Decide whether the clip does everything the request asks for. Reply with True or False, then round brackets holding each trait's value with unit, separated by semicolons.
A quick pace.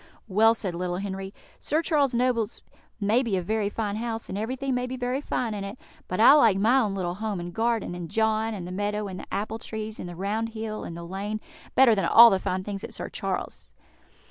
True (230 wpm)